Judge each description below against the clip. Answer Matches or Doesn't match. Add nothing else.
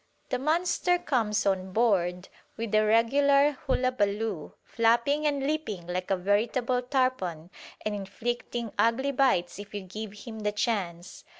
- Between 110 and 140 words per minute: Matches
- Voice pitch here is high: Matches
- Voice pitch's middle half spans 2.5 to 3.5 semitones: Doesn't match